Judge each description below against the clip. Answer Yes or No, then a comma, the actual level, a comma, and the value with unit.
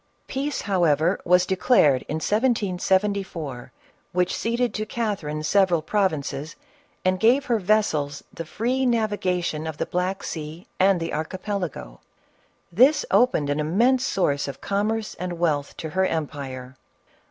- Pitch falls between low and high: Yes, medium, 180 Hz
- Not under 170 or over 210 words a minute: No, average, 140 wpm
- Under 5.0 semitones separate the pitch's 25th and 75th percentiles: No, wide, 5.6 semitones